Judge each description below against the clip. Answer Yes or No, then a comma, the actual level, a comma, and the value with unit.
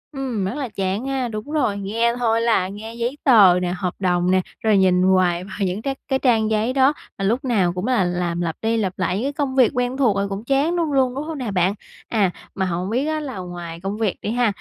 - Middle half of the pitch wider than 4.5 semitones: Yes, wide, 5.4 semitones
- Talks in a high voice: Yes, high, 215 Hz